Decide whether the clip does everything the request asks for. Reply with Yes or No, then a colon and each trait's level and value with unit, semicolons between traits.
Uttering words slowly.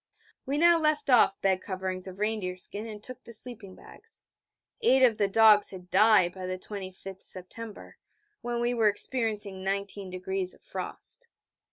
No: average, 160 wpm